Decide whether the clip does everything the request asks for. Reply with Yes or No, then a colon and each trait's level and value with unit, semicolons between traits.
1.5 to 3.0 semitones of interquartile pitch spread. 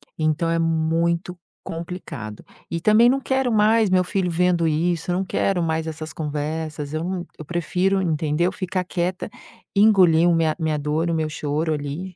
Yes: narrow, 2.6 semitones